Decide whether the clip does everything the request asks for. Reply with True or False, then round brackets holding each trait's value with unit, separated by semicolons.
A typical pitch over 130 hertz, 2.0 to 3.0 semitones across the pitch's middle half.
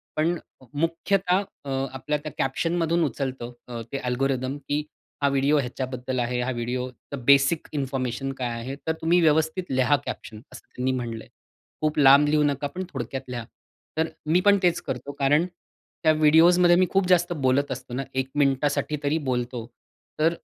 False (140 Hz; 3.7 semitones)